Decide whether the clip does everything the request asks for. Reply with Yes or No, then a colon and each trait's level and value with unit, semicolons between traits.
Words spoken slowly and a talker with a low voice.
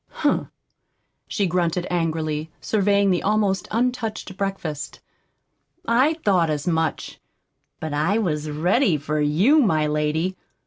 No: slow, 120 wpm; medium, 175 Hz